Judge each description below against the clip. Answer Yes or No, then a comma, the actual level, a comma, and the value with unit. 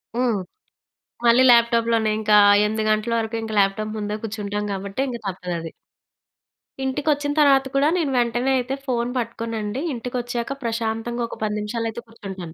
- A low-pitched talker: No, high, 230 Hz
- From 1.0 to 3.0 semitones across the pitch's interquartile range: Yes, narrow, 2.5 semitones